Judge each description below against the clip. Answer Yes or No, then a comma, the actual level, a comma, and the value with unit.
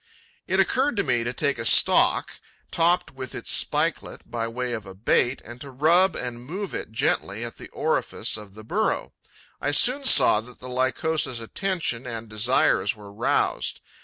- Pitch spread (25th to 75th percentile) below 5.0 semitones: No, wide, 5.4 semitones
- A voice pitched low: Yes, low, 125 Hz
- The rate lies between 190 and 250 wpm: No, average, 175 wpm